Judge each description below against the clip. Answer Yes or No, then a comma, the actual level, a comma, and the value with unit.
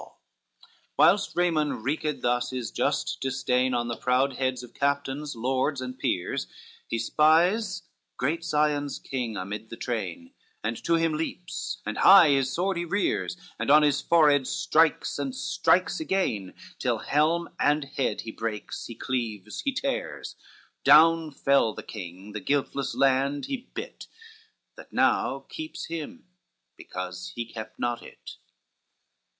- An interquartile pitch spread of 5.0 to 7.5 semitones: Yes, wide, 5.4 semitones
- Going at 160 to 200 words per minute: No, average, 145 wpm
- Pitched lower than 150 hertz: Yes, medium, 140 Hz